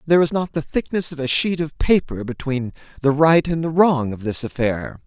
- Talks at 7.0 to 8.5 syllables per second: No, 5.2 syllables/s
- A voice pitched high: No, medium, 145 Hz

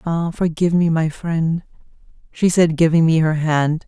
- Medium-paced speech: Yes, average, 155 wpm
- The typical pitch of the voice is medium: Yes, medium, 165 Hz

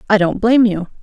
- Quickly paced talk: Yes, fast, 235 wpm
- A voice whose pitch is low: No, high, 210 Hz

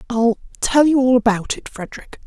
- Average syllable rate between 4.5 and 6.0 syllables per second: Yes, 5.5 syllables/s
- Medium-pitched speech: No, high, 240 Hz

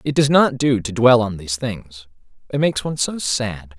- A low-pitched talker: Yes, low, 120 Hz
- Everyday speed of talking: No, fast, 220 wpm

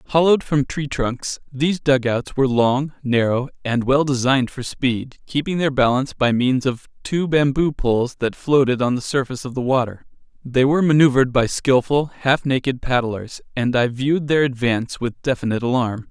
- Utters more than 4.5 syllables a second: Yes, 5.3 syllables/s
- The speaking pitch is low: Yes, low, 130 Hz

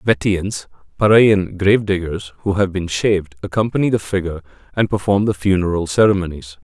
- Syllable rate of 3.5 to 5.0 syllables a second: Yes, 4.9 syllables/s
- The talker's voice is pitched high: No, very low, 95 Hz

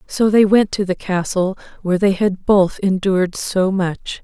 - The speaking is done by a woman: Yes, female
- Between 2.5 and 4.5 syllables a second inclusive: Yes, 4.4 syllables/s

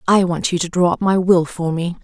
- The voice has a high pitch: No, medium, 175 Hz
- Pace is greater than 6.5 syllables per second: No, 5.5 syllables/s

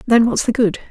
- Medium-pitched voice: No, high, 225 Hz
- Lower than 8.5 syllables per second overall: Yes, 5.9 syllables/s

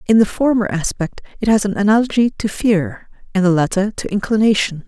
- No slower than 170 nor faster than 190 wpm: Yes, average, 185 wpm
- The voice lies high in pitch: Yes, high, 205 Hz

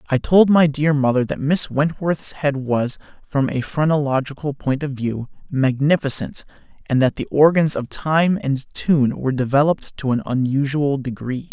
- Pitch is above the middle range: No, medium, 140 Hz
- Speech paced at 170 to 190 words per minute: No, average, 160 wpm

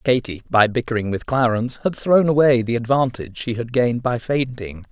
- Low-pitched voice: Yes, low, 120 Hz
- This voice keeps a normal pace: Yes, average, 185 wpm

